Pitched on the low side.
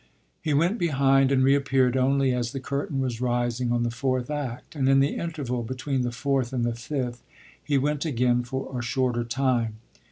Yes: low, 130 Hz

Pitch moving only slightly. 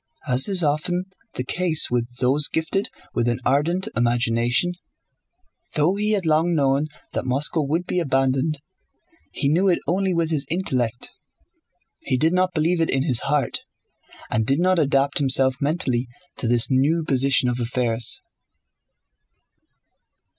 No: average, 4.8 semitones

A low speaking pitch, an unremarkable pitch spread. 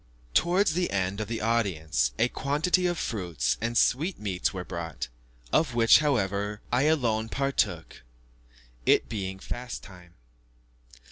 No: low, 115 Hz; wide, 6.6 semitones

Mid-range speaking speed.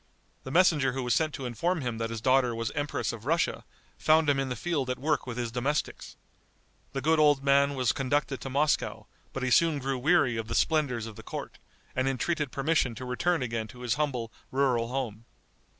No: fast, 210 wpm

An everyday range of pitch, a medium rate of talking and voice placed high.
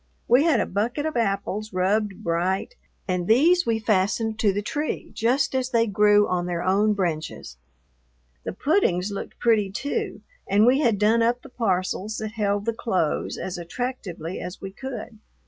Yes: average, 4.0 semitones; average, 170 wpm; high, 210 Hz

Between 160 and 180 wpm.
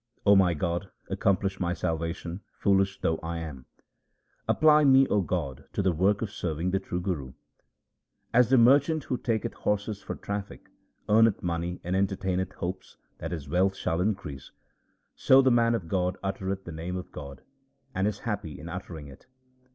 Yes: average, 170 wpm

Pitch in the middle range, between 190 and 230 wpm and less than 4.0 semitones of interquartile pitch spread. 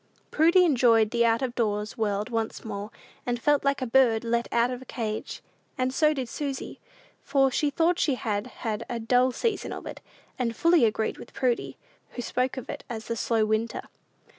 No: high, 240 Hz; average, 195 wpm; average, 3.0 semitones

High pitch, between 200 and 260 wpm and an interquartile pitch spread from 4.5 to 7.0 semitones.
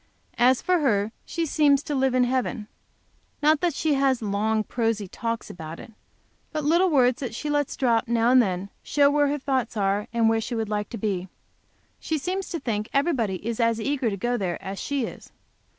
Yes: high, 240 Hz; fast, 205 wpm; average, 4.9 semitones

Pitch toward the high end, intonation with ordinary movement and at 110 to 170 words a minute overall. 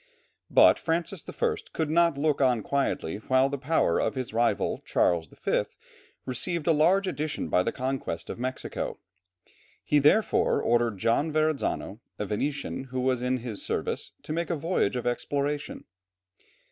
No: low, 135 Hz; average, 4.6 semitones; average, 155 wpm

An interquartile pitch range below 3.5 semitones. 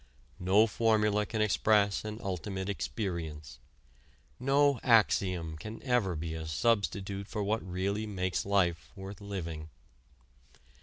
Yes: average, 3.1 semitones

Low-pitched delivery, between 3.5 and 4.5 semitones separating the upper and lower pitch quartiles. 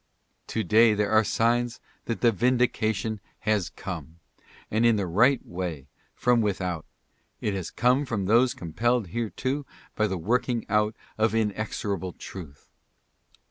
Yes: low, 110 Hz; average, 3.8 semitones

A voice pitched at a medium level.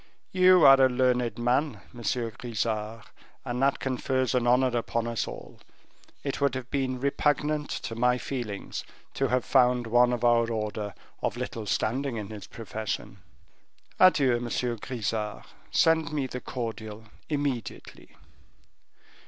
No: low, 125 Hz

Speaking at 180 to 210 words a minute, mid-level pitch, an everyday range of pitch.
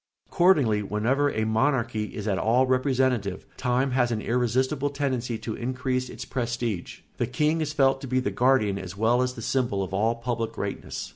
No: average, 185 wpm; low, 125 Hz; average, 3.0 semitones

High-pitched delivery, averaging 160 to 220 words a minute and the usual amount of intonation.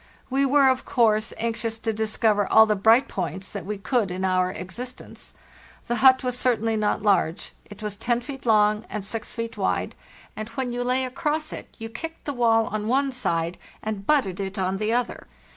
Yes: high, 225 Hz; average, 195 wpm; average, 3.6 semitones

